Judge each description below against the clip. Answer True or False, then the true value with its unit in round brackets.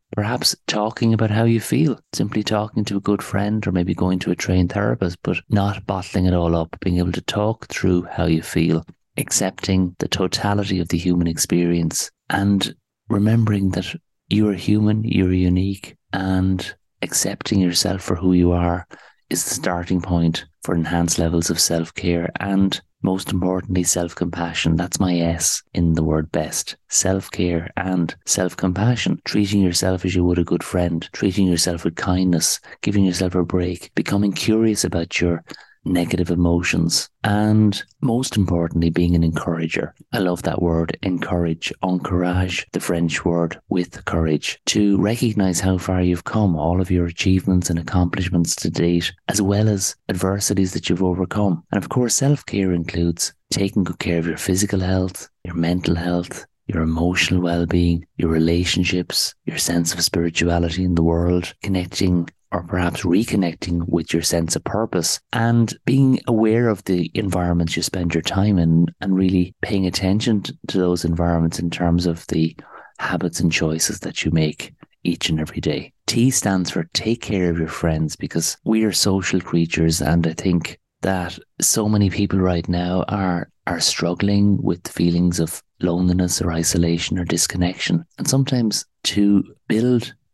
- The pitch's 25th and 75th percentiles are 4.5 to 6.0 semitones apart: False (2.6 semitones)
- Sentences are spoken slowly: False (165 wpm)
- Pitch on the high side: False (90 Hz)